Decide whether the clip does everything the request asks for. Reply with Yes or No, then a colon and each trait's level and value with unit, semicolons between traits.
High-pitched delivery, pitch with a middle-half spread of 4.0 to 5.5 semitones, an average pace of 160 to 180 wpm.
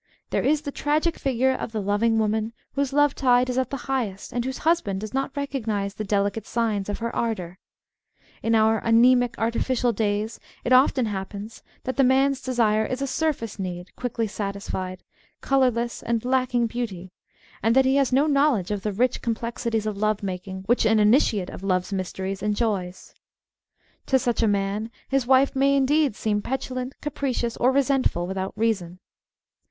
Yes: high, 230 Hz; average, 4.3 semitones; average, 175 wpm